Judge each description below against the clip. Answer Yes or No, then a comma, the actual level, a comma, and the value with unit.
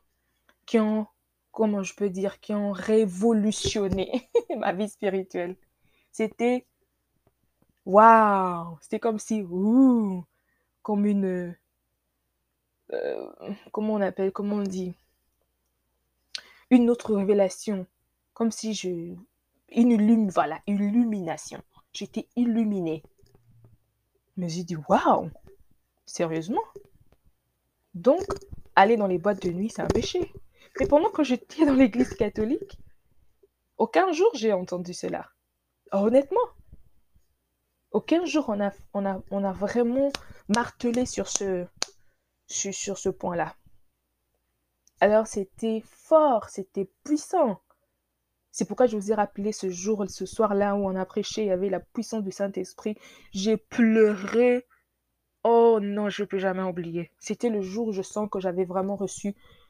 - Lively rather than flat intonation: No, average, 3.7 semitones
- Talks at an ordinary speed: No, slow, 130 wpm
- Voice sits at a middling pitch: No, high, 205 Hz